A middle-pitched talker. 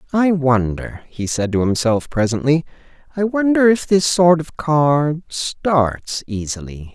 Yes: medium, 145 Hz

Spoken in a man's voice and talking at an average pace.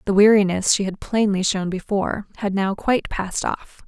No: female; average, 185 wpm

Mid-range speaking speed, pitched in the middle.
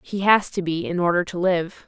No: fast, 255 wpm; medium, 180 Hz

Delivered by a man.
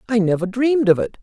Yes: male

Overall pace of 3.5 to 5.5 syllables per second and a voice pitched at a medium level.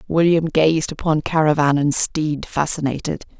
Yes: 4.5 syllables/s; medium, 155 Hz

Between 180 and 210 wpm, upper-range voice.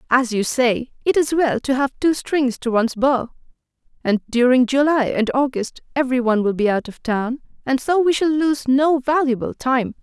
Yes: average, 190 wpm; very high, 260 Hz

